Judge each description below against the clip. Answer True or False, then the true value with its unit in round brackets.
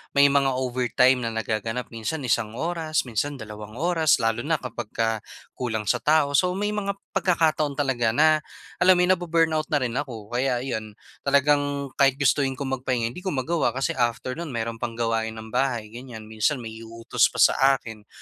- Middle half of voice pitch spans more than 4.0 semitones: True (4.4 semitones)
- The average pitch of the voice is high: False (130 Hz)